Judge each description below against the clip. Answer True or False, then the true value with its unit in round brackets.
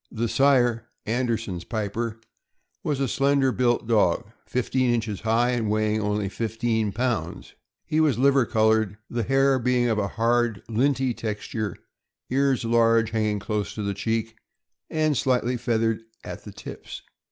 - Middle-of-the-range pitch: False (115 Hz)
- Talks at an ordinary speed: True (150 wpm)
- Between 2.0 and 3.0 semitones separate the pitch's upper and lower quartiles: True (2.6 semitones)